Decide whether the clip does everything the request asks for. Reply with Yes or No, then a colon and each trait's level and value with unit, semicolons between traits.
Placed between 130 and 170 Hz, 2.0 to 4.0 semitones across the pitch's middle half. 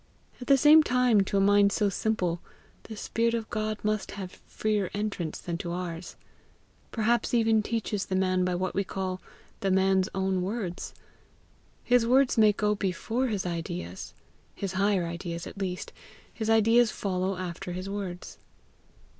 No: high, 195 Hz; average, 3.2 semitones